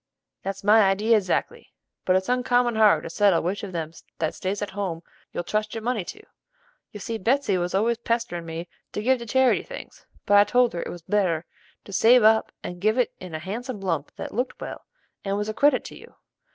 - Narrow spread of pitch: No, average, 4.0 semitones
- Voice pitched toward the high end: Yes, high, 205 Hz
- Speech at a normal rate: No, fast, 220 wpm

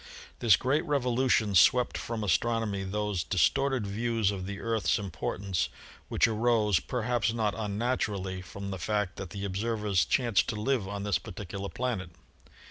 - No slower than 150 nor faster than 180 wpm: Yes, average, 155 wpm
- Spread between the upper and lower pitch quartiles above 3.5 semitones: No, average, 3.2 semitones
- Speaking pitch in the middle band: No, low, 105 Hz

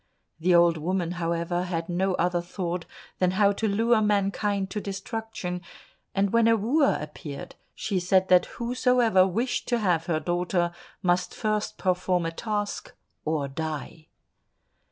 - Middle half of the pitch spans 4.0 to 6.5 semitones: No, average, 3.4 semitones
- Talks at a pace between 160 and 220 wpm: No, average, 145 wpm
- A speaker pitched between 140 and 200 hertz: Yes, medium, 185 Hz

